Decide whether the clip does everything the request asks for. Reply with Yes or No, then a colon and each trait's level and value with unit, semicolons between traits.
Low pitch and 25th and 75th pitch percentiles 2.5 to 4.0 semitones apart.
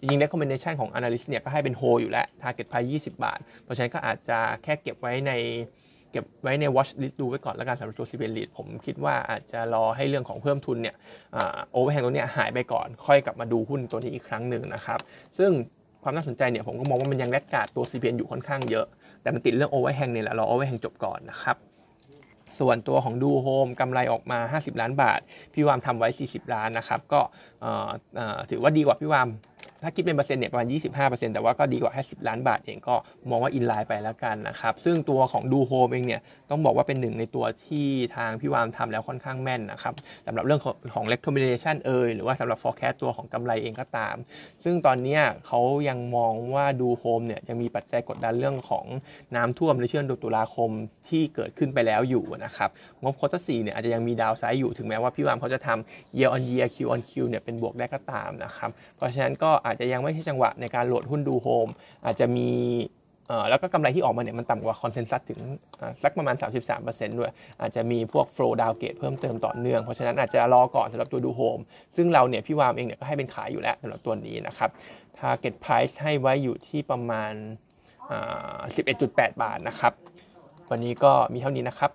Yes: low, 125 Hz; average, 3.2 semitones